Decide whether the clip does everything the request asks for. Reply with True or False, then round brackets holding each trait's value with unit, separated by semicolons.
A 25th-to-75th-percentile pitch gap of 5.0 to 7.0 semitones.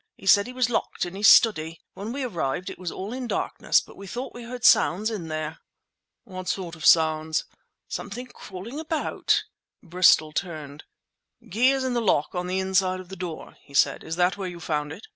True (5.5 semitones)